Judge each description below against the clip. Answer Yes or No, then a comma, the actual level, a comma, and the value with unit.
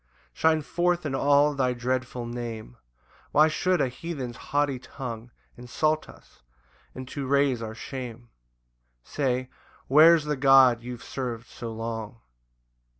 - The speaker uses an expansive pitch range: No, average, 3.4 semitones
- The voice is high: No, low, 130 Hz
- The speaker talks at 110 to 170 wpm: Yes, slow, 135 wpm